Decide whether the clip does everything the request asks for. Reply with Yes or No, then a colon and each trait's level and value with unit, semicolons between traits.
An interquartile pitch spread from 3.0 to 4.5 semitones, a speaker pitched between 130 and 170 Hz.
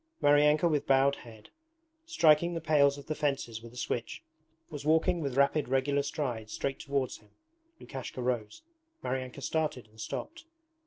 Yes: average, 3.3 semitones; medium, 140 Hz